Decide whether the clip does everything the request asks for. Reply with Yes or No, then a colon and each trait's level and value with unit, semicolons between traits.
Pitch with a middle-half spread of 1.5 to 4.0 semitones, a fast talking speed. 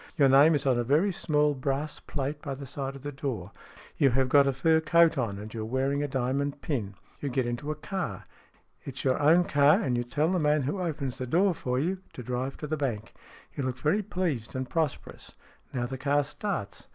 Yes: average, 2.9 semitones; fast, 235 wpm